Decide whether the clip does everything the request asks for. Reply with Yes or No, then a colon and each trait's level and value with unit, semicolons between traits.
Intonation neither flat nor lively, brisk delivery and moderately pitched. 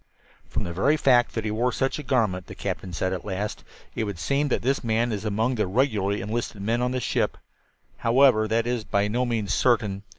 No: average, 3.5 semitones; fast, 220 wpm; low, 115 Hz